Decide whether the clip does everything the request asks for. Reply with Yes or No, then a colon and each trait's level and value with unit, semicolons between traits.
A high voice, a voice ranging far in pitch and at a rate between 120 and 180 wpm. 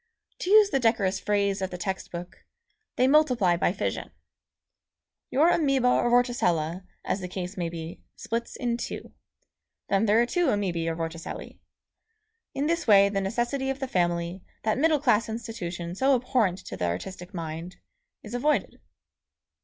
Yes: high, 205 Hz; wide, 6.0 semitones; average, 160 wpm